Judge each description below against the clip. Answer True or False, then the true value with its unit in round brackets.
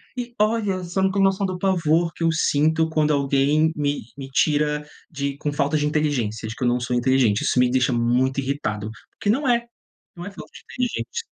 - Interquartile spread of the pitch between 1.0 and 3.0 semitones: False (5.3 semitones)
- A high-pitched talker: False (150 Hz)